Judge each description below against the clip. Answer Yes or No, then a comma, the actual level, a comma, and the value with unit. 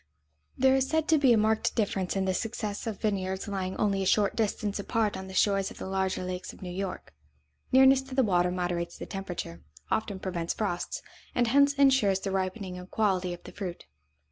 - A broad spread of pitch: No, average, 3.2 semitones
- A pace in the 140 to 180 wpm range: No, fast, 205 wpm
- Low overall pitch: No, high, 195 Hz